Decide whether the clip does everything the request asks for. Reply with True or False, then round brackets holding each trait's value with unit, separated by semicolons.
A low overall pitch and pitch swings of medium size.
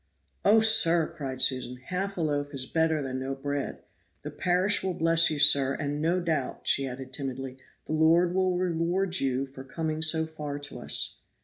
False (155 Hz; 4.1 semitones)